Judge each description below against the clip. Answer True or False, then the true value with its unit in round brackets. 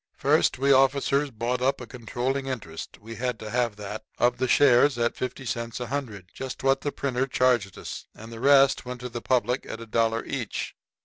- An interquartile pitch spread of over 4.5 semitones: False (2.7 semitones)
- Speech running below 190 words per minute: False (205 wpm)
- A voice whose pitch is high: False (125 Hz)